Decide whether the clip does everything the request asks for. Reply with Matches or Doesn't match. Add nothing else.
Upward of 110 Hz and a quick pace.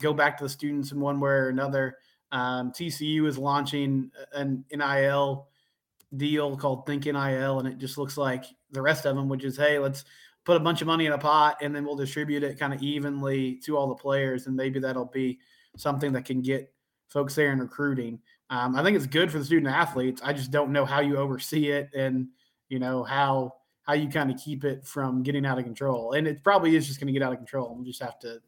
Matches